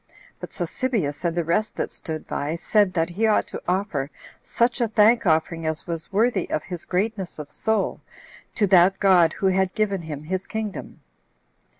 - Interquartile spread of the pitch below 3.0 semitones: No, average, 4.5 semitones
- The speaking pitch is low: No, medium, 185 Hz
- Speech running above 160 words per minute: Yes, average, 180 wpm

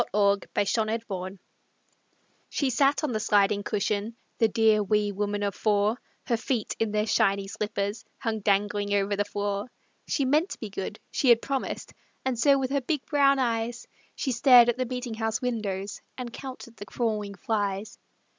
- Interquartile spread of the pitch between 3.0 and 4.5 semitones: Yes, average, 3.3 semitones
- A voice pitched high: Yes, high, 220 Hz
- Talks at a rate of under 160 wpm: No, average, 175 wpm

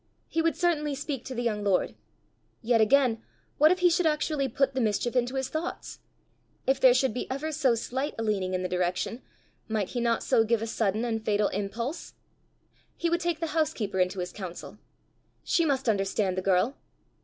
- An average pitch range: No, wide, 5.7 semitones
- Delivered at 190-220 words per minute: Yes, average, 195 wpm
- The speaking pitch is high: Yes, high, 240 Hz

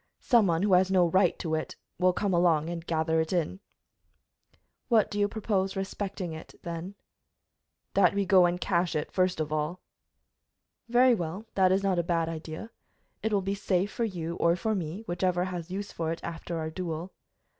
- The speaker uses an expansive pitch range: No, average, 2.9 semitones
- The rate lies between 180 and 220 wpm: Yes, average, 190 wpm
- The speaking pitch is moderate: Yes, medium, 180 Hz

